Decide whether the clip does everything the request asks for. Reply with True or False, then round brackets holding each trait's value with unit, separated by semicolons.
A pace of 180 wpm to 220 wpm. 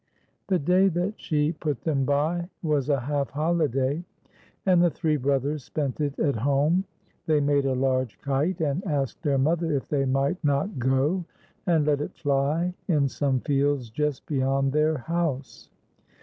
False (165 wpm)